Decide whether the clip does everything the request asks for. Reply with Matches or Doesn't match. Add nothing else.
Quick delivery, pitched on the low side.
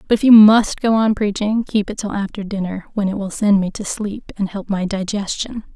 Doesn't match